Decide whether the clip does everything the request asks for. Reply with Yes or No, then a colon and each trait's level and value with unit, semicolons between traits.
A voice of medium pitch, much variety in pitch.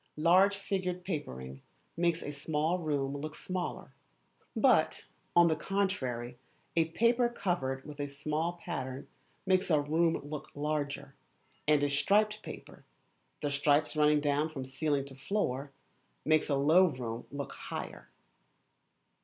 No: medium, 150 Hz; average, 3.7 semitones